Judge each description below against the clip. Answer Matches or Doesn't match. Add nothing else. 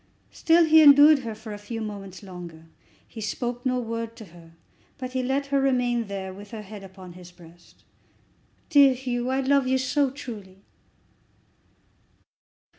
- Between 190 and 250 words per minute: Doesn't match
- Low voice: Doesn't match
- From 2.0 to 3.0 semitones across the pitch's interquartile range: Doesn't match